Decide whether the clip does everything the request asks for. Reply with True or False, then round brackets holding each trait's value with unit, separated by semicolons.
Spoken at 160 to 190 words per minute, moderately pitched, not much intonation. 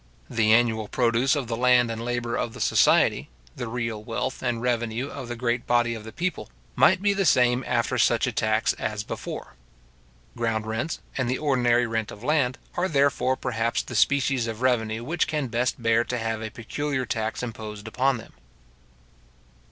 False (185 wpm; 120 Hz; 2.3 semitones)